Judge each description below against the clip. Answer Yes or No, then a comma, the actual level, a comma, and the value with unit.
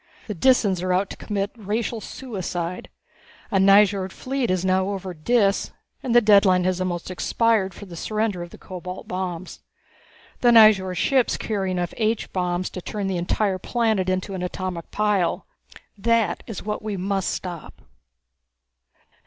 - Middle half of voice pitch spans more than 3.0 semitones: No, average, 2.7 semitones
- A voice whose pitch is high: Yes, high, 195 Hz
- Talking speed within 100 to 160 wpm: Yes, average, 155 wpm